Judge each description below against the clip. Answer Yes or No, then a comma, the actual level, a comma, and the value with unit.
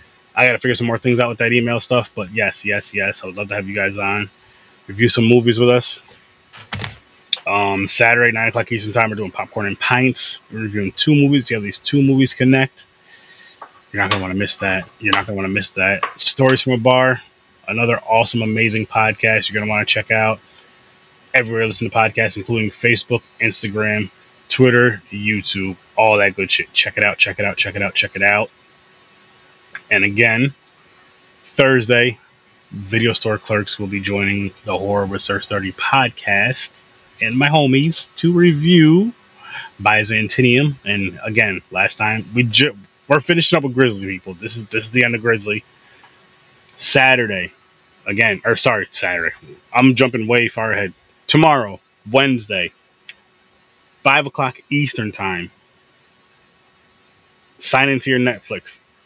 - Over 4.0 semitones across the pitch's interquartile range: No, average, 3.6 semitones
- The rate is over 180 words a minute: No, average, 170 wpm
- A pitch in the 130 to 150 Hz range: No, low, 115 Hz